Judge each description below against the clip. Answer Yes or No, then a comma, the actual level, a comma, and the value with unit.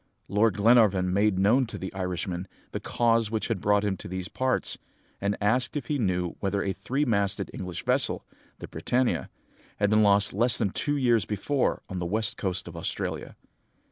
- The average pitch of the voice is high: No, low, 105 Hz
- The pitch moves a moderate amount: Yes, average, 3.6 semitones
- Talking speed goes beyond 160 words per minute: Yes, average, 185 wpm